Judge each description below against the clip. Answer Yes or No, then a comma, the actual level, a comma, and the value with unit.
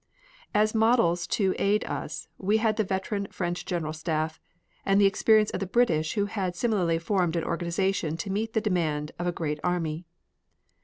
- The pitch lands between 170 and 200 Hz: Yes, medium, 185 Hz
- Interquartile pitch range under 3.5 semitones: No, average, 3.9 semitones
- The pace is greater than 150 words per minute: Yes, average, 175 wpm